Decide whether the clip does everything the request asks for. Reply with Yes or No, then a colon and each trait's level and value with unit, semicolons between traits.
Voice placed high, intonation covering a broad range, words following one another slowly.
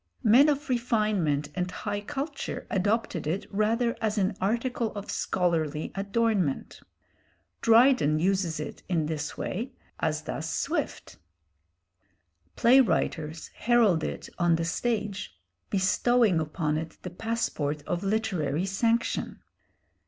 Yes: high, 195 Hz; wide, 6.1 semitones; slow, 115 wpm